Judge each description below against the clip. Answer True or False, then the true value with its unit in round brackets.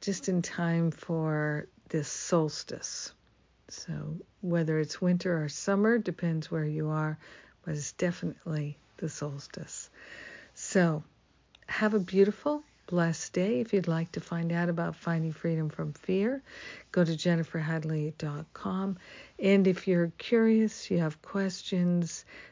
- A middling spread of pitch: True (3.1 semitones)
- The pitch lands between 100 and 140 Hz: False (170 Hz)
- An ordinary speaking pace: False (130 wpm)